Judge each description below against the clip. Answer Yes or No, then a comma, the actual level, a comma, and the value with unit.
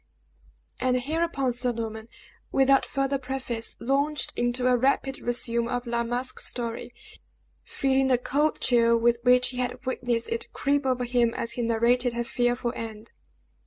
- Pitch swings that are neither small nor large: No, narrow, 2.1 semitones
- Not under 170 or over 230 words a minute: No, average, 155 wpm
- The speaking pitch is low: No, high, 245 Hz